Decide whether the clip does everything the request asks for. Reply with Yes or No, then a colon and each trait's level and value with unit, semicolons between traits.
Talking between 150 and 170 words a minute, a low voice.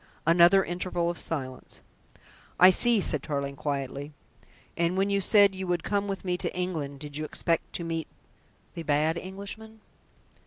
No: average, 160 wpm; medium, 170 Hz